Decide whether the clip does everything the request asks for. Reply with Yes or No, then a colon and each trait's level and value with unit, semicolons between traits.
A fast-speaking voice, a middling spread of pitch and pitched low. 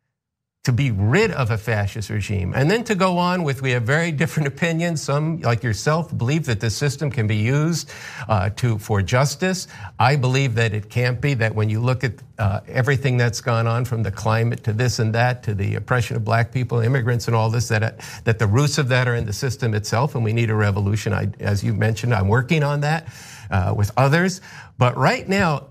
Yes: fast, 215 wpm; average, 4.2 semitones; low, 120 Hz